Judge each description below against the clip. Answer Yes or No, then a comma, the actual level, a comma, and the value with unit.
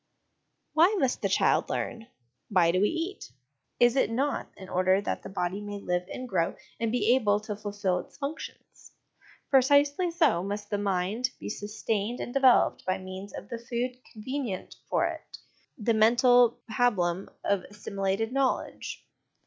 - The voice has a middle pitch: No, high, 215 Hz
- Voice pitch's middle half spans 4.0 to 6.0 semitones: Yes, average, 4.4 semitones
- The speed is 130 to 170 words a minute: Yes, average, 155 wpm